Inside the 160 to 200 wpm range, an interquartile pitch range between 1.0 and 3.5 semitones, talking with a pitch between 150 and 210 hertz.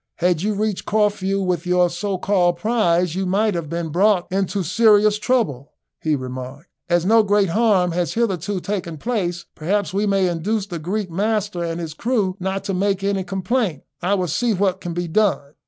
Yes: average, 190 wpm; average, 3.2 semitones; high, 190 Hz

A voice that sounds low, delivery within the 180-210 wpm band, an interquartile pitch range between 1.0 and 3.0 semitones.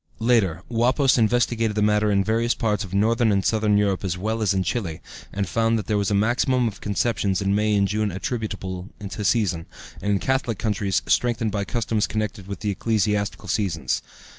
Yes: low, 105 Hz; average, 190 wpm; narrow, 2.4 semitones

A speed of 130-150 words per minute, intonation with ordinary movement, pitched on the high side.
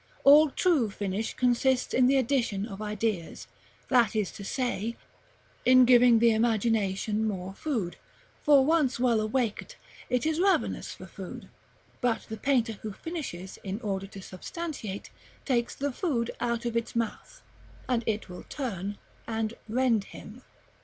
Yes: average, 145 wpm; average, 3.6 semitones; high, 230 Hz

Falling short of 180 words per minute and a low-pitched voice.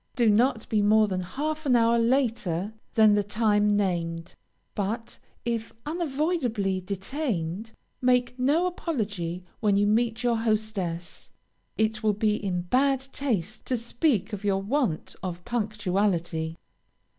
No: slow, 135 wpm; high, 215 Hz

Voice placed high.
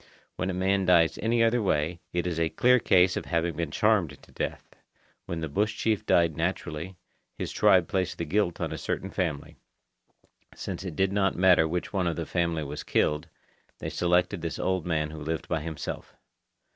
No: very low, 85 Hz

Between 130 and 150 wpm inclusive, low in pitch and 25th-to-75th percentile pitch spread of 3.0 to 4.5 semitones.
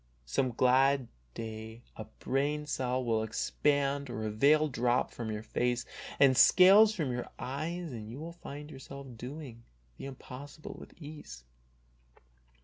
Yes: average, 145 wpm; low, 130 Hz; average, 3.9 semitones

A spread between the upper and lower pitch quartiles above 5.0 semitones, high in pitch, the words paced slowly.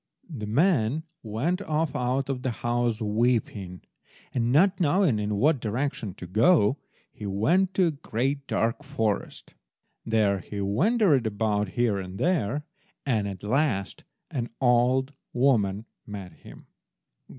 No: wide, 5.5 semitones; low, 120 Hz; slow, 130 wpm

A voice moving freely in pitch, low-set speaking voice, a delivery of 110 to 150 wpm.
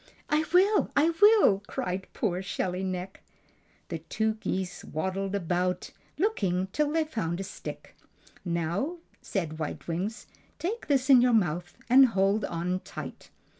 No: wide, 6.9 semitones; high, 195 Hz; average, 140 wpm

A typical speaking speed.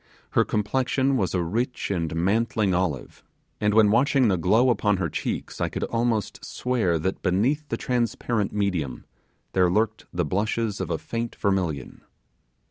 Yes: average, 155 wpm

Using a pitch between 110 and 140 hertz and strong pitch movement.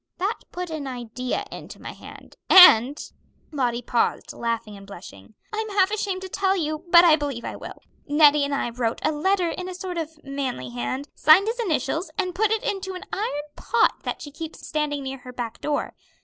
No: very high, 300 Hz; wide, 6.6 semitones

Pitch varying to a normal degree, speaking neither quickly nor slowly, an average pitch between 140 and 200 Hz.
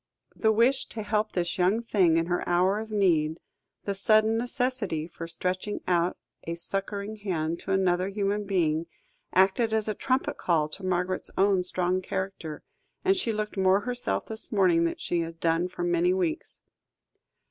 Yes: average, 3.5 semitones; average, 170 wpm; high, 190 Hz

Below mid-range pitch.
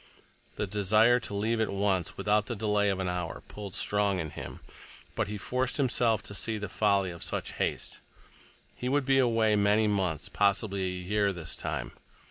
Yes: low, 105 Hz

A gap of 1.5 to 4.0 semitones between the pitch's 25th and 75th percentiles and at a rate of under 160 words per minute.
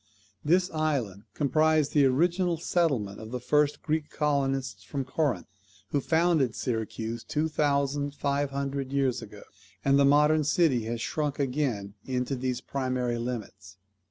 Yes: average, 3.3 semitones; average, 140 wpm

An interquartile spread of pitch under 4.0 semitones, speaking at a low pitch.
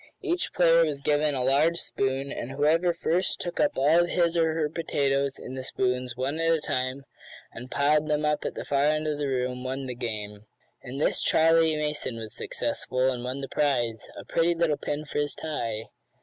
No: average, 3.6 semitones; medium, 145 Hz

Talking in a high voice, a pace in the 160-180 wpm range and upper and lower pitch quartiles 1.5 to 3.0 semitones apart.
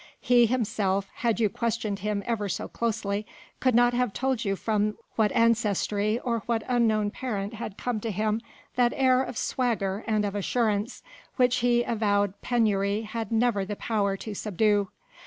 Yes: high, 220 Hz; average, 165 wpm; narrow, 2.6 semitones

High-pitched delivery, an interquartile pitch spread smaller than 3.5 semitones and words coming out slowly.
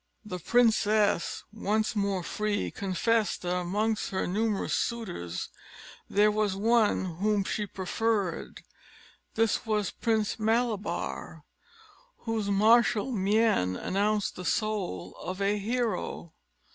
Yes: high, 210 Hz; narrow, 2.5 semitones; slow, 105 wpm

